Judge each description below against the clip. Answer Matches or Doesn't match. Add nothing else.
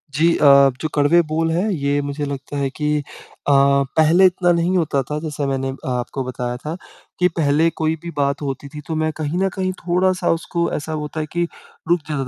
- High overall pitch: Doesn't match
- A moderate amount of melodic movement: Matches